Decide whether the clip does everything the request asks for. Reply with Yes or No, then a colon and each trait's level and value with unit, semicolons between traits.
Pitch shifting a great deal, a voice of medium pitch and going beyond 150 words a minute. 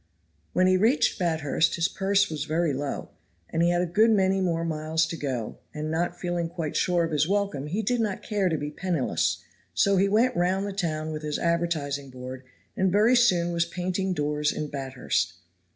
No: average, 3.8 semitones; medium, 170 Hz; average, 200 wpm